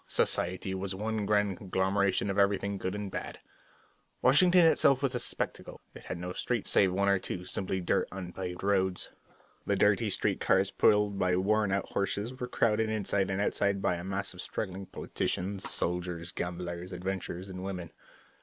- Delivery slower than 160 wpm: No, average, 175 wpm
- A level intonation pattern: Yes, narrow, 2.0 semitones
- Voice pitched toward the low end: Yes, very low, 95 Hz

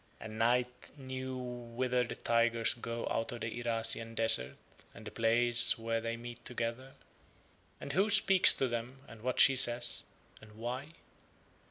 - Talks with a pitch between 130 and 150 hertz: No, low, 120 Hz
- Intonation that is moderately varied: No, narrow, 1.7 semitones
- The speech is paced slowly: No, average, 155 wpm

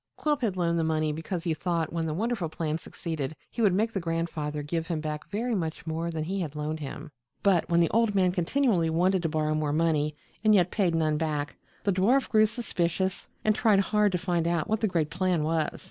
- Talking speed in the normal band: No, fast, 225 wpm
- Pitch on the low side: No, medium, 170 Hz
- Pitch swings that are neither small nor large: Yes, average, 3.8 semitones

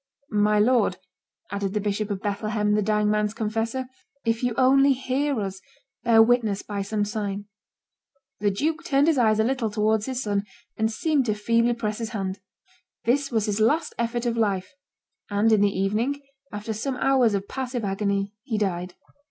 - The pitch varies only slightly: No, average, 3.0 semitones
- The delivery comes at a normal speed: Yes, average, 175 wpm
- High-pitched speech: Yes, high, 220 Hz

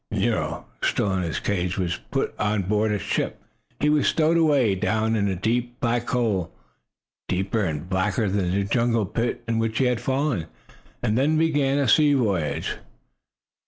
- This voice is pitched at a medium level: No, low, 110 Hz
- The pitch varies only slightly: No, average, 4.7 semitones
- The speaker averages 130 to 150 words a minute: No, average, 170 wpm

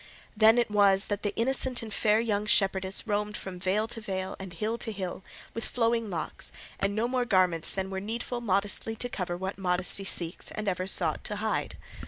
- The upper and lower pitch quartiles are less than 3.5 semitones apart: Yes, average, 2.9 semitones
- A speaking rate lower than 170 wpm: No, average, 200 wpm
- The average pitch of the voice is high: Yes, high, 205 Hz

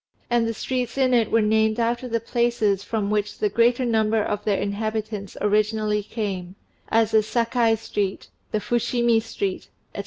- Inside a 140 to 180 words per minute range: Yes, average, 165 wpm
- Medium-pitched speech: No, high, 220 Hz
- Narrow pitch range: Yes, narrow, 1.9 semitones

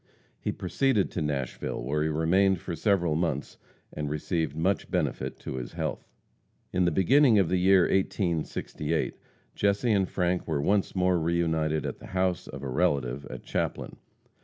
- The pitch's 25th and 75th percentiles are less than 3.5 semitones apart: No, average, 3.9 semitones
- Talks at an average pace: Yes, average, 165 wpm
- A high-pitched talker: No, very low, 85 Hz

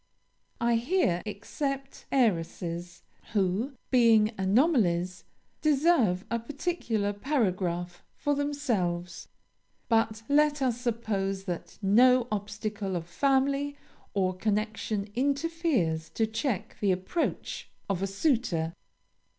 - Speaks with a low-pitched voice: No, high, 220 Hz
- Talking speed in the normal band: No, slow, 100 wpm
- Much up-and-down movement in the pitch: Yes, wide, 6.4 semitones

